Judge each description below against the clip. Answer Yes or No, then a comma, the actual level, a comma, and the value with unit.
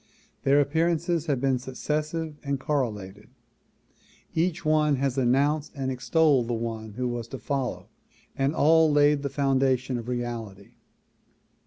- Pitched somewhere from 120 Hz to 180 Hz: Yes, low, 135 Hz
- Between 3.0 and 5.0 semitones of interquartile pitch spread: Yes, average, 3.7 semitones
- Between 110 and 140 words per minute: Yes, slow, 135 wpm